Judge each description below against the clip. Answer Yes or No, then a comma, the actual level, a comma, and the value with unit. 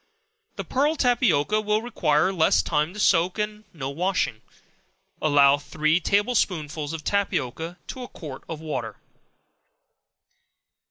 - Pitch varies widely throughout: Yes, wide, 6.0 semitones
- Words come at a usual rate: No, slow, 125 wpm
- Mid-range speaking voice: Yes, medium, 165 Hz